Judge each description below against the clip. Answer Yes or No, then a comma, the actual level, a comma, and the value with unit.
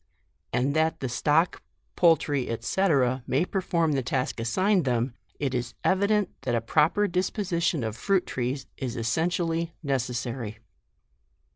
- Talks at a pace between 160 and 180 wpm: No, average, 140 wpm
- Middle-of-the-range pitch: Yes, medium, 145 Hz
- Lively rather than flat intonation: Yes, wide, 6.1 semitones